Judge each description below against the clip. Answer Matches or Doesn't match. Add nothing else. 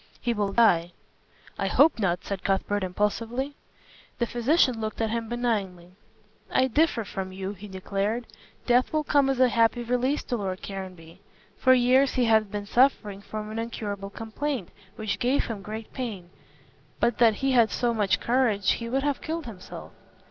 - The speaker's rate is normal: Matches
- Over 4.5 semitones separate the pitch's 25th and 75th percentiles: Doesn't match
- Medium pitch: Doesn't match